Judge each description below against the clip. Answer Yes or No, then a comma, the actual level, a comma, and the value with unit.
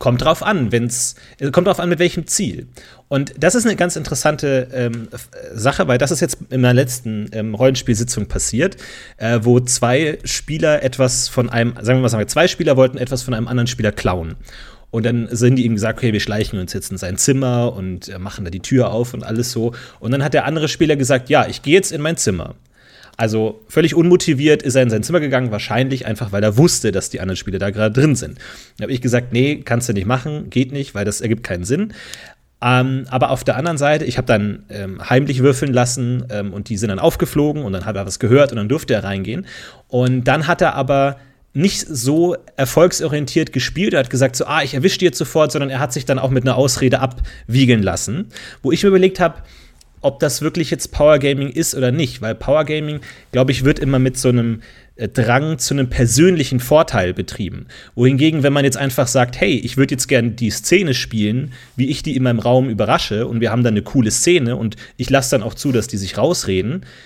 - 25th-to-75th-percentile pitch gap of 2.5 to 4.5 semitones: Yes, average, 4.2 semitones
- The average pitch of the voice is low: Yes, low, 130 Hz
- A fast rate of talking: Yes, fast, 220 wpm